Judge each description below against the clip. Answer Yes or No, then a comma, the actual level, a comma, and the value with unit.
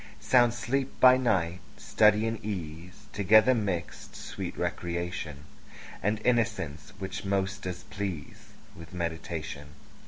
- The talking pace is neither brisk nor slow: No, slow, 115 wpm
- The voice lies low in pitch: Yes, very low, 95 Hz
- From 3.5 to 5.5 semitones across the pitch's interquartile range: Yes, average, 4.6 semitones